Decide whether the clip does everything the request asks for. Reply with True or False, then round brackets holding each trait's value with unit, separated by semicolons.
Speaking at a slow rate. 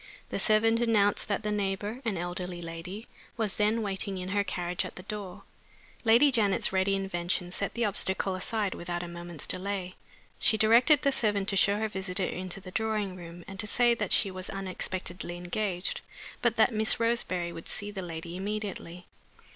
False (180 wpm)